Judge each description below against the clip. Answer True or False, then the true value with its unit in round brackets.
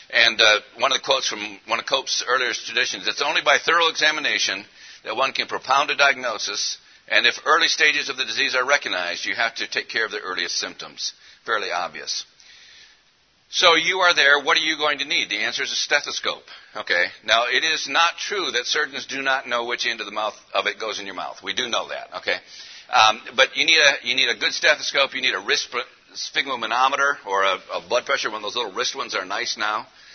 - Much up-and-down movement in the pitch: False (3.9 semitones)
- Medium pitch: True (150 Hz)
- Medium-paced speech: False (230 wpm)